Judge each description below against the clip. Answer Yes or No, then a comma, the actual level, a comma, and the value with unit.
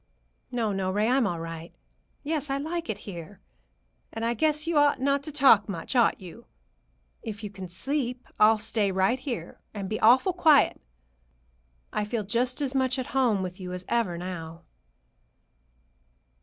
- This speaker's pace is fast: No, average, 170 wpm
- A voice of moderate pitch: No, high, 225 Hz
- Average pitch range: No, wide, 5.9 semitones